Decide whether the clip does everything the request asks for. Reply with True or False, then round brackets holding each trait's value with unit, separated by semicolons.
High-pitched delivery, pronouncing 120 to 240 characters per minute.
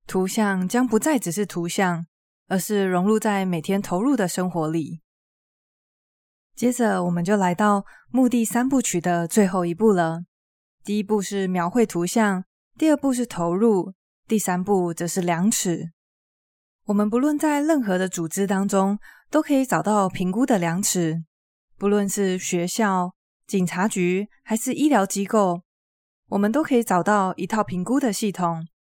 True (195 Hz; 230 characters per minute)